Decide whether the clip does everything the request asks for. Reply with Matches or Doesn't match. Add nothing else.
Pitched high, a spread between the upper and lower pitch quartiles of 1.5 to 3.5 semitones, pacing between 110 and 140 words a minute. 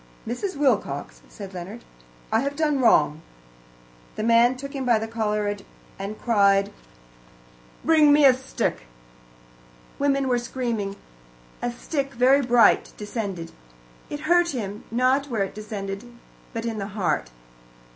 Doesn't match